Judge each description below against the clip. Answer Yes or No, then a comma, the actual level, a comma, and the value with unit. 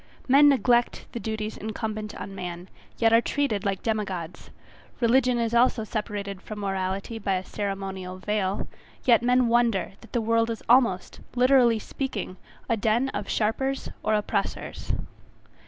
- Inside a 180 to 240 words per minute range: No, average, 150 wpm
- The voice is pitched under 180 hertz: No, high, 220 Hz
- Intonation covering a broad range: No, average, 3.3 semitones